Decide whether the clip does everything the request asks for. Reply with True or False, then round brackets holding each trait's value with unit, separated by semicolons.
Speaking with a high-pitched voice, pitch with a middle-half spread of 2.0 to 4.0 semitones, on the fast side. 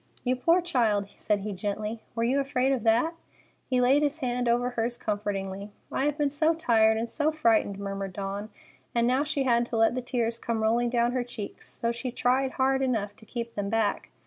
True (235 Hz; 3.4 semitones; 210 wpm)